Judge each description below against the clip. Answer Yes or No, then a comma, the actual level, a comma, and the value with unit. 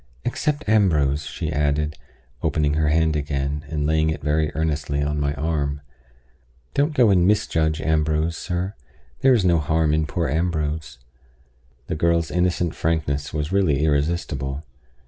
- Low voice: Yes, very low, 80 Hz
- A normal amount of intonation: No, narrow, 2.3 semitones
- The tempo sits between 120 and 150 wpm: Yes, average, 145 wpm